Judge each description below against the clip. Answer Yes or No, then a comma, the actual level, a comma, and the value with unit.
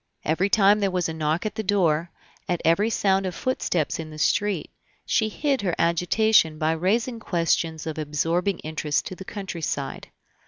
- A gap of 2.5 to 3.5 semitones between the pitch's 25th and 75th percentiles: No, average, 4.1 semitones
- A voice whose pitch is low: No, medium, 175 Hz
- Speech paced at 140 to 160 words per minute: No, average, 170 wpm